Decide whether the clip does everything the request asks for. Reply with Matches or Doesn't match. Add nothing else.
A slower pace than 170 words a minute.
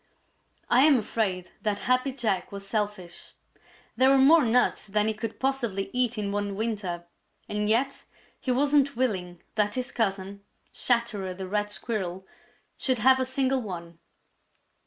Matches